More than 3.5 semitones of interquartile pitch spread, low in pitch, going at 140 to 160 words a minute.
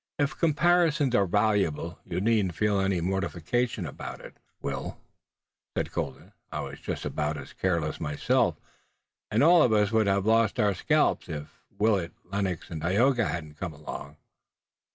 Yes: average, 5.1 semitones; low, 100 Hz; average, 155 wpm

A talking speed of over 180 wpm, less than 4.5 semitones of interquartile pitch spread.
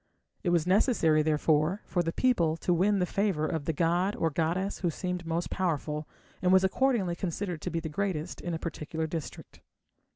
Yes: average, 190 wpm; average, 2.9 semitones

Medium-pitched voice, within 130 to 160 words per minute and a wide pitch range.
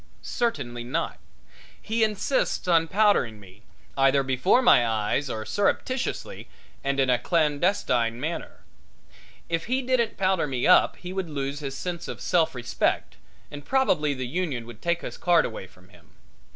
Yes: medium, 150 Hz; average, 155 wpm; wide, 7.0 semitones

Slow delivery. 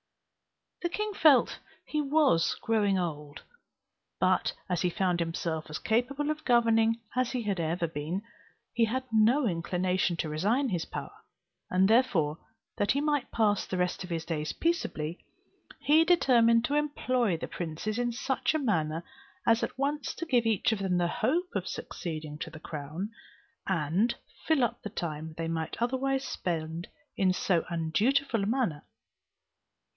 No: average, 160 wpm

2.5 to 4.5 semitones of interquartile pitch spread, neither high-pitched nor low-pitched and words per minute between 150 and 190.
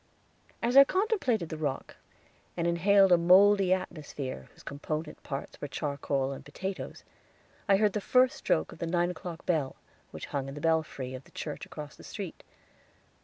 No: average, 5.2 semitones; medium, 170 Hz; average, 170 wpm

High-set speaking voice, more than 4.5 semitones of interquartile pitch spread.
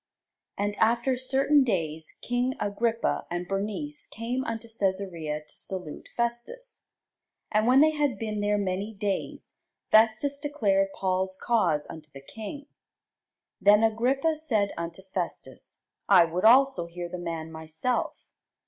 Yes: high, 210 Hz; wide, 5.4 semitones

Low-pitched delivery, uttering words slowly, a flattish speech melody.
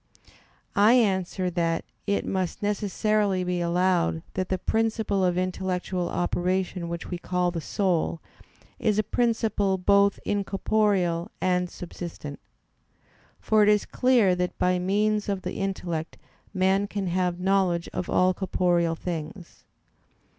No: medium, 185 Hz; slow, 130 wpm; narrow, 2.2 semitones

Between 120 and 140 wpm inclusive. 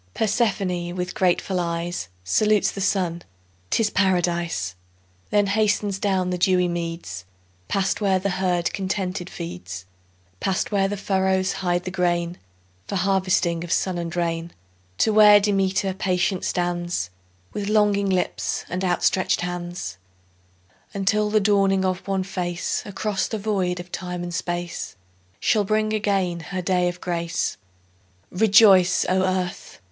Yes: slow, 135 wpm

